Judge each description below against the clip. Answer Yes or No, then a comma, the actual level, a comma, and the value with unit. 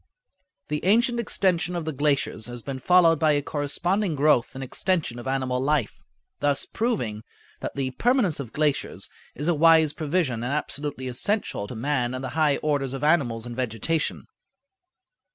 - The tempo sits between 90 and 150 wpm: No, average, 165 wpm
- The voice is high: No, medium, 145 Hz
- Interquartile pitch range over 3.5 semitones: Yes, average, 4.3 semitones